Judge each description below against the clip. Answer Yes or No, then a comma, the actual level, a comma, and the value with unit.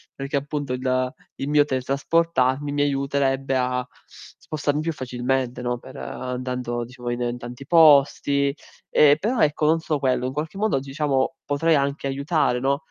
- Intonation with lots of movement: No, narrow, 2.4 semitones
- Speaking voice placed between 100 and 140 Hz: Yes, low, 135 Hz